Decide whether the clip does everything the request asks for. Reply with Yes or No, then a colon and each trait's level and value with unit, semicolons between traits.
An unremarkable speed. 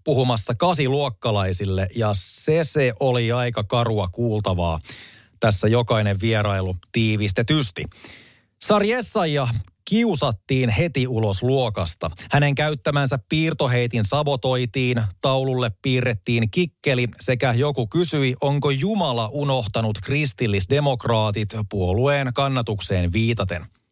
No: slow, 90 wpm